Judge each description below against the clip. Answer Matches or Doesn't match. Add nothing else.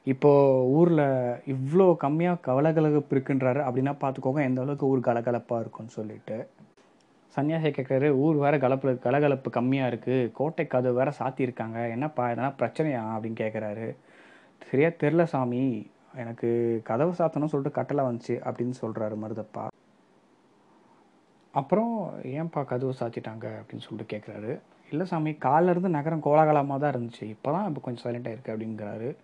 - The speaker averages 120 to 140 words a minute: Matches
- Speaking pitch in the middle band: Doesn't match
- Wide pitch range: Doesn't match